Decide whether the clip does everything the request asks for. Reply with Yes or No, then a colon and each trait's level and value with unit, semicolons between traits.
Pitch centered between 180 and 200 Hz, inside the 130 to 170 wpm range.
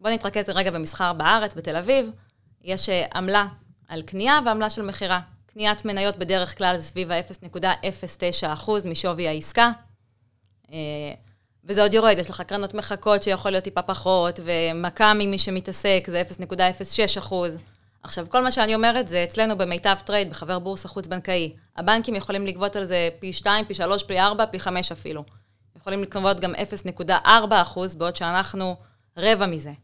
Yes: medium, 185 Hz; average, 145 wpm